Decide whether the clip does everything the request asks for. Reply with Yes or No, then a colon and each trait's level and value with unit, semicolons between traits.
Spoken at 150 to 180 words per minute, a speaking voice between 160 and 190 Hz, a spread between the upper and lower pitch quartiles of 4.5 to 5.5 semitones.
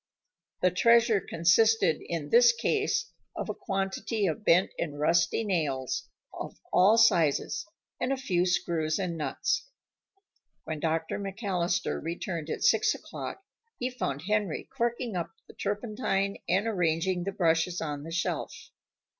No: average, 140 wpm; medium, 185 Hz; average, 4.8 semitones